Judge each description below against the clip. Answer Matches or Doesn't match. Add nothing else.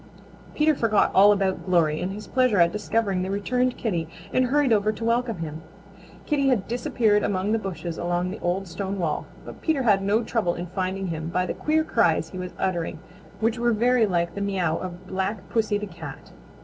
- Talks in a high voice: Matches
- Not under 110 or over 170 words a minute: Doesn't match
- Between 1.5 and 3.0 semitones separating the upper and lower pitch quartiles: Doesn't match